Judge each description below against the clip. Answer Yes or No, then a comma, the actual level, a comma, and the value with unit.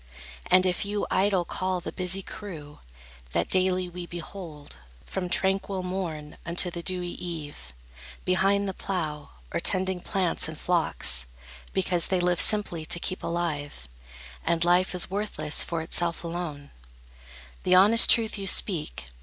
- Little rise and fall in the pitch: Yes, narrow, 2.2 semitones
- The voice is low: No, medium, 180 Hz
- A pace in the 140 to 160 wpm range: Yes, average, 145 wpm